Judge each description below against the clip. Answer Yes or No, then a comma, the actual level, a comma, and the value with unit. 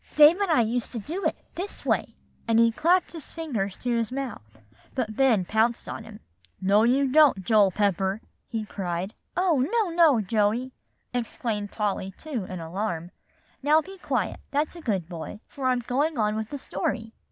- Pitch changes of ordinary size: No, wide, 5.9 semitones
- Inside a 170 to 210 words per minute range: Yes, average, 180 wpm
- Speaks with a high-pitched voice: Yes, high, 230 Hz